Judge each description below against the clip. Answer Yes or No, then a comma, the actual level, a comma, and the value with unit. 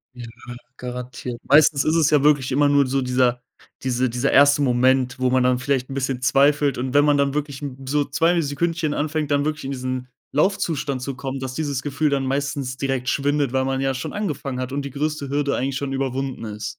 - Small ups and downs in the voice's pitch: Yes, narrow, 2.1 semitones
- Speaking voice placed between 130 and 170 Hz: Yes, low, 135 Hz